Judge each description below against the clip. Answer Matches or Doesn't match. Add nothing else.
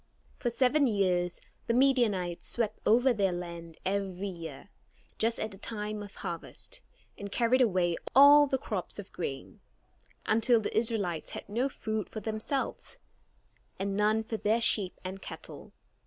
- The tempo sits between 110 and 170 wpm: Matches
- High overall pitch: Matches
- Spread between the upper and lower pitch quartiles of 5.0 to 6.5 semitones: Doesn't match